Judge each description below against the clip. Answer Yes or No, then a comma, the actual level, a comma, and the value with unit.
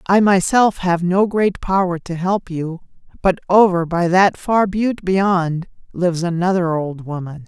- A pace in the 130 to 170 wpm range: Yes, average, 160 wpm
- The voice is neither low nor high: Yes, medium, 180 Hz